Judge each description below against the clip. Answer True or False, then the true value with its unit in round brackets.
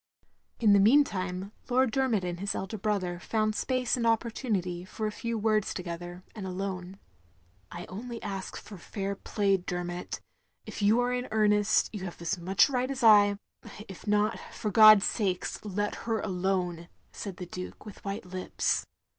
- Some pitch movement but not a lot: True (3.1 semitones)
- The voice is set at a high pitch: True (200 Hz)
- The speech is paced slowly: False (170 wpm)